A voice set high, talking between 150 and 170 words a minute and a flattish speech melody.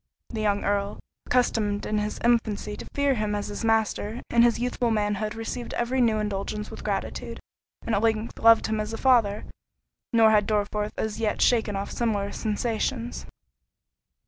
Yes: high, 220 Hz; average, 165 wpm; narrow, 2.0 semitones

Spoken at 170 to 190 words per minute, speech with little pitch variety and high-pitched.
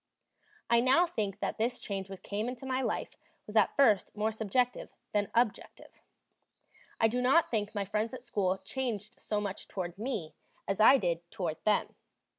No: average, 175 wpm; average, 3.9 semitones; high, 215 Hz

